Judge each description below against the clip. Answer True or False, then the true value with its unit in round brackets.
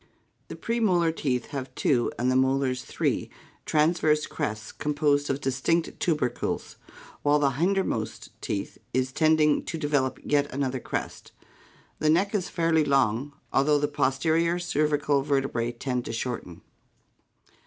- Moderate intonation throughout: True (3.4 semitones)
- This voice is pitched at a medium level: True (145 Hz)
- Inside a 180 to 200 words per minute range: False (140 wpm)